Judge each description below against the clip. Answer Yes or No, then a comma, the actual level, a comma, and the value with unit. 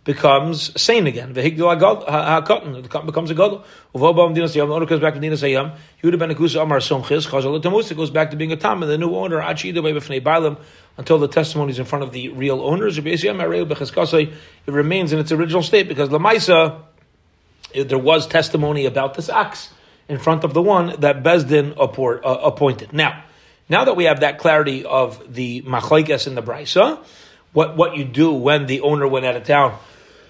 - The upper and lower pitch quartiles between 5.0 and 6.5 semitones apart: No, average, 2.9 semitones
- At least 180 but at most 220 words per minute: No, average, 155 wpm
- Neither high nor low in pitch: Yes, medium, 155 Hz